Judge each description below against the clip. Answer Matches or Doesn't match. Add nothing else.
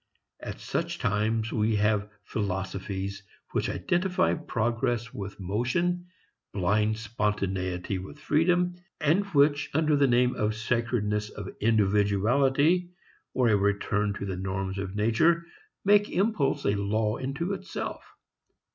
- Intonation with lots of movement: Matches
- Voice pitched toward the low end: Matches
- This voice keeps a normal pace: Doesn't match